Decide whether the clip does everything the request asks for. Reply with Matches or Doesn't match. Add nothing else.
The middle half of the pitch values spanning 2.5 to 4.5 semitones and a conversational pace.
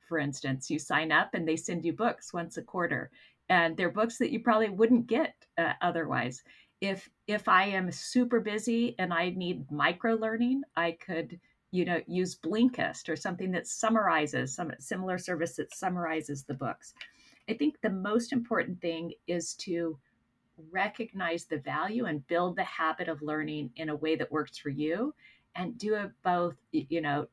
Doesn't match